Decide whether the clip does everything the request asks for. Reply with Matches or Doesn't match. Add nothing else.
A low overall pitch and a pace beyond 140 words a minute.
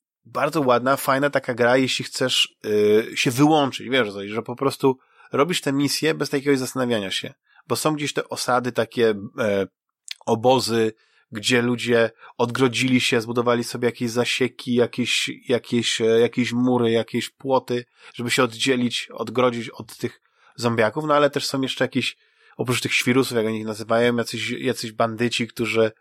Matches